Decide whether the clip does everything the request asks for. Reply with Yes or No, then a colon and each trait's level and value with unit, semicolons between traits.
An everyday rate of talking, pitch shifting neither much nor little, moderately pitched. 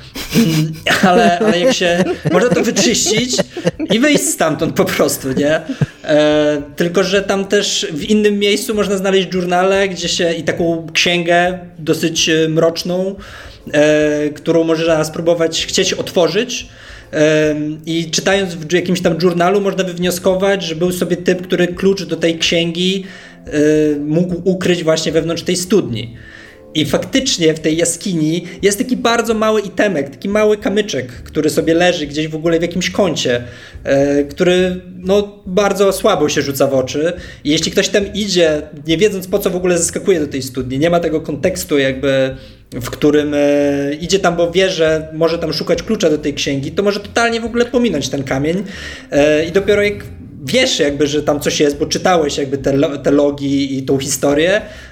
No: fast, 165 wpm; average, 4.2 semitones; medium, 170 Hz